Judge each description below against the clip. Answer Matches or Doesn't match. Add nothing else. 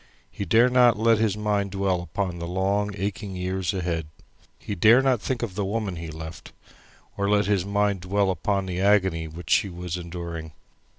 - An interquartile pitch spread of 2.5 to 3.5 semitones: Matches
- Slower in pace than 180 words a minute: Doesn't match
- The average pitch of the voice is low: Matches